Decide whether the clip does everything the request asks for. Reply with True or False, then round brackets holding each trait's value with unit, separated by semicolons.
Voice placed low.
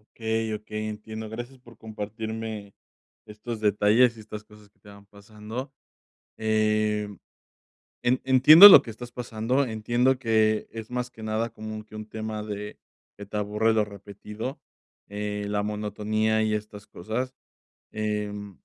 True (110 Hz)